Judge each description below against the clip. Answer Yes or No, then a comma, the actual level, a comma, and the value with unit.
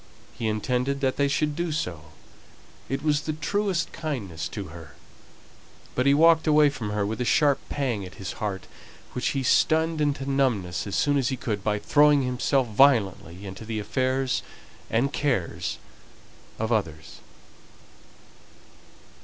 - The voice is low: Yes, low, 130 Hz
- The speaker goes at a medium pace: Yes, average, 150 wpm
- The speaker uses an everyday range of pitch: No, wide, 5.8 semitones